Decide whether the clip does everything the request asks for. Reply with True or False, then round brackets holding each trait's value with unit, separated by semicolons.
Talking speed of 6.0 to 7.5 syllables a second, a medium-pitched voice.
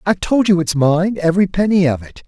True (6.1 syllables/s; 175 Hz)